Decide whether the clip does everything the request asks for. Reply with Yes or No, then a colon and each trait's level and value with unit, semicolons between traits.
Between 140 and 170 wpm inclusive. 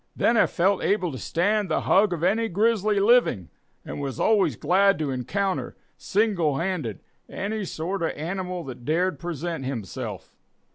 Yes: average, 160 wpm